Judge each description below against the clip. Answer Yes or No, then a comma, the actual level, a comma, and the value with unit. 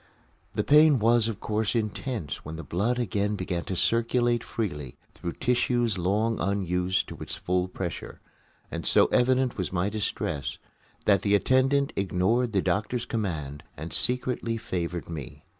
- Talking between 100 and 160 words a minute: Yes, average, 150 wpm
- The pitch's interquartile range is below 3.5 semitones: No, average, 5.0 semitones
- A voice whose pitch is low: Yes, low, 105 Hz